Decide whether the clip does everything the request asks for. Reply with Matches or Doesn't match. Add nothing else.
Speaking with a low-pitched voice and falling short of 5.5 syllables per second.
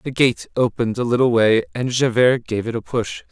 Matches